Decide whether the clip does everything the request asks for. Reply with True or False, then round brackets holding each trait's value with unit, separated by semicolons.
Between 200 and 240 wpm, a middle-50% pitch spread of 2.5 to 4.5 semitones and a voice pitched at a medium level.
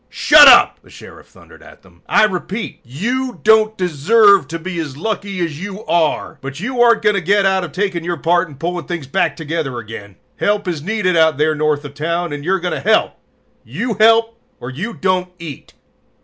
False (205 wpm; 5.3 semitones; 180 Hz)